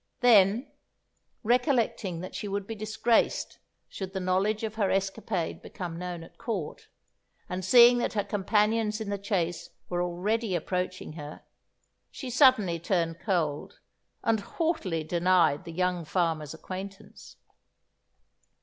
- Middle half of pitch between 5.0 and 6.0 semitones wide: No, average, 3.9 semitones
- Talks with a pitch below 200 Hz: Yes, high, 190 Hz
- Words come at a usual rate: No, slow, 130 wpm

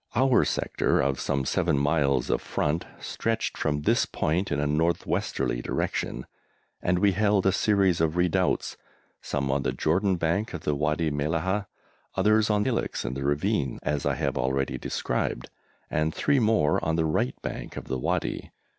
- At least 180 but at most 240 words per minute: No, average, 170 wpm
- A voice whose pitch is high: No, very low, 80 Hz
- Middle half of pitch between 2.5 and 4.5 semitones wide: No, average, 5.3 semitones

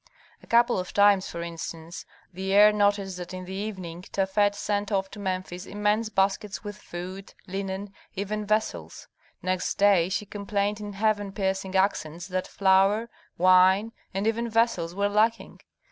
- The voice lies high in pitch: Yes, high, 195 Hz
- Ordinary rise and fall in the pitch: No, narrow, 2.0 semitones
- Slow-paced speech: No, average, 155 wpm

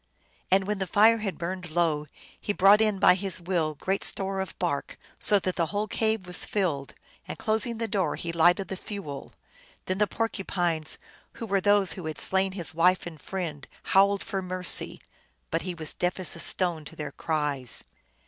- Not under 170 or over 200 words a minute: Yes, average, 190 wpm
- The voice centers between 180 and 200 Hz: Yes, medium, 185 Hz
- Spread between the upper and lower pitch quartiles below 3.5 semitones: Yes, average, 3.0 semitones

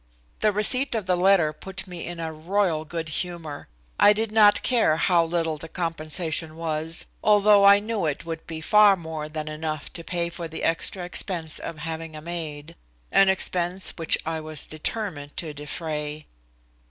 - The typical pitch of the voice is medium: Yes, medium, 165 Hz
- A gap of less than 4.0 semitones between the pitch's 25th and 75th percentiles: Yes, average, 3.4 semitones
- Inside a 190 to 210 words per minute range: No, average, 170 wpm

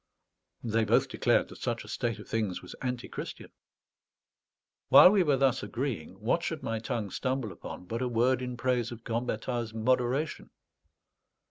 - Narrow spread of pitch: Yes, narrow, 2.3 semitones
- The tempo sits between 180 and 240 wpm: No, average, 155 wpm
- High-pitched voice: No, low, 120 Hz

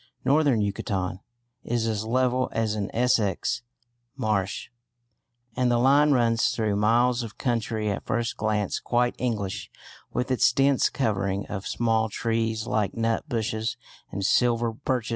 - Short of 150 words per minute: Yes, average, 140 wpm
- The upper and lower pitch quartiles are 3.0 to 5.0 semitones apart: No, narrow, 2.5 semitones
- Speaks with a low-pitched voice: Yes, low, 115 Hz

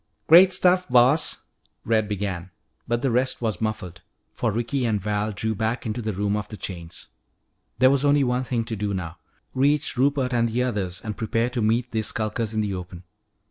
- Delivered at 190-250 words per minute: Yes, average, 200 wpm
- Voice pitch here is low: Yes, low, 110 Hz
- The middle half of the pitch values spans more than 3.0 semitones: Yes, average, 3.5 semitones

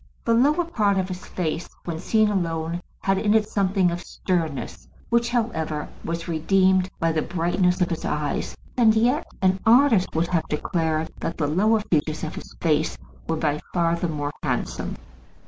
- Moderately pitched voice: Yes, medium, 180 Hz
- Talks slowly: No, average, 175 wpm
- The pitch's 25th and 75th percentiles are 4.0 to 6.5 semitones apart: Yes, average, 4.5 semitones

